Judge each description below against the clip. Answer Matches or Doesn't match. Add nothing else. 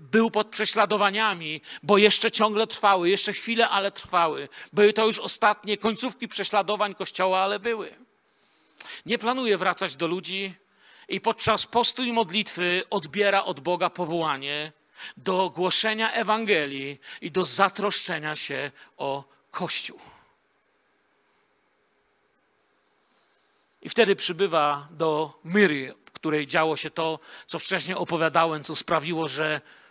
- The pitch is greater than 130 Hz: Matches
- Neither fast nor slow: Matches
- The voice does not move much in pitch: Doesn't match